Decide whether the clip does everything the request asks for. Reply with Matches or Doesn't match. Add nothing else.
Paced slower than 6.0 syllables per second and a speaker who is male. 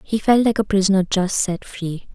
Doesn't match